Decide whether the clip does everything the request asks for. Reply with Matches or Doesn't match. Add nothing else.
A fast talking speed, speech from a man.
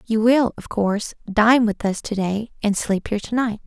Doesn't match